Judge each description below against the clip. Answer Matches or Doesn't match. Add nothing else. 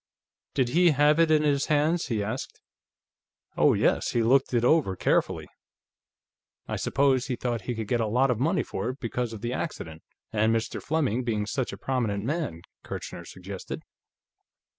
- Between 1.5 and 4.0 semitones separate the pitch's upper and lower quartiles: Doesn't match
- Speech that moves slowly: Doesn't match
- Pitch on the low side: Matches